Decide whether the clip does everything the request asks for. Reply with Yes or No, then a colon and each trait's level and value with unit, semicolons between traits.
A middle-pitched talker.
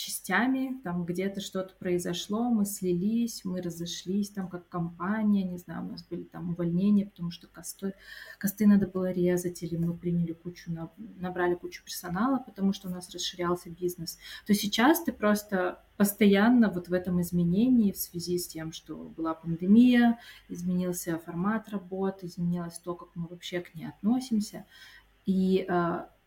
Yes: medium, 180 Hz